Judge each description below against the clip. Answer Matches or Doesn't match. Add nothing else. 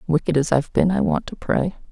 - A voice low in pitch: Doesn't match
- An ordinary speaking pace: Doesn't match